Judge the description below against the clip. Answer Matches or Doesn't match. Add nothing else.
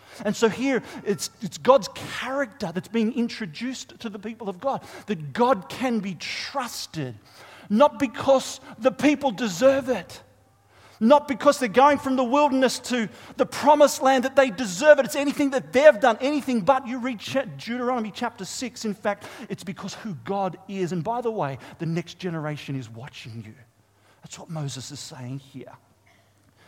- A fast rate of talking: Doesn't match